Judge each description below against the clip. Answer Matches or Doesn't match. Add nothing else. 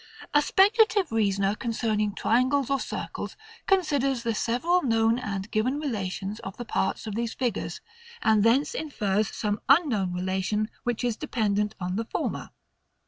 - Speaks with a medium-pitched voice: Doesn't match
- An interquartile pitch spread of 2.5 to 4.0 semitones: Doesn't match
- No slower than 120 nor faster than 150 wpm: Matches